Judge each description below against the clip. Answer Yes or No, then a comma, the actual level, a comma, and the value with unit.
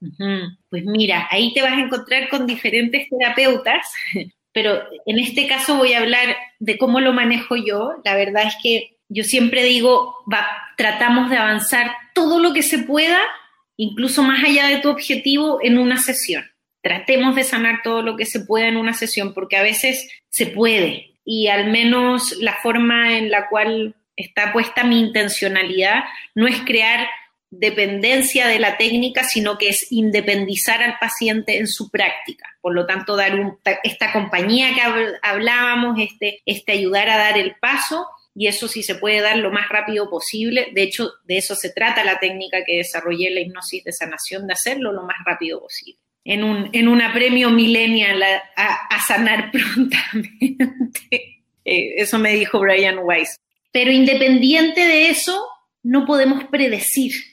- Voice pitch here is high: Yes, high, 230 Hz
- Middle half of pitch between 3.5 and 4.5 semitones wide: Yes, average, 3.8 semitones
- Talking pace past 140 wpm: Yes, average, 165 wpm